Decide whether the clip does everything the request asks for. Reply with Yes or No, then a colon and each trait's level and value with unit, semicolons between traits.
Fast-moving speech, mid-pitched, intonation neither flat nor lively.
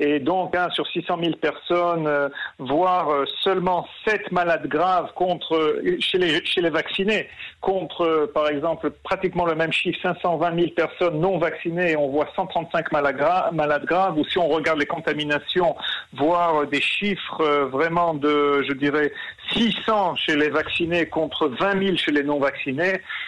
No: average, 165 wpm; medium, 170 Hz; average, 3.4 semitones